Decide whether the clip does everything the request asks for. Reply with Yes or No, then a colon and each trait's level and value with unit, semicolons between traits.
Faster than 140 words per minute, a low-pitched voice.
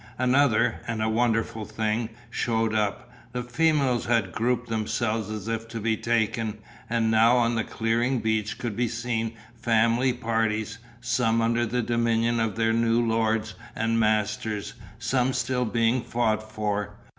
Yes: average, 150 wpm; low, 115 Hz